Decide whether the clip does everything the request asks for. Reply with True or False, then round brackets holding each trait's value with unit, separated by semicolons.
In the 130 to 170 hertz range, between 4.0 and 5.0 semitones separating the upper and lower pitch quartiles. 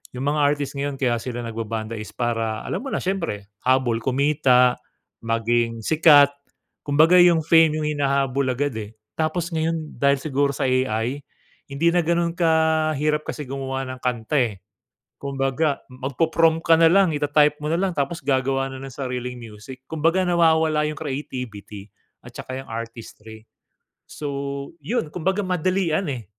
True (140 Hz; 4.4 semitones)